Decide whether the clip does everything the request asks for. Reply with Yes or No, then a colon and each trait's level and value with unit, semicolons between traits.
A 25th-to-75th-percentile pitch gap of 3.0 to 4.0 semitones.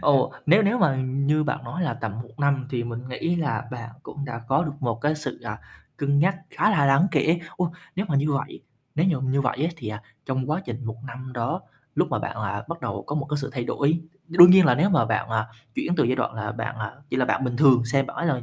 No: average, 4.5 semitones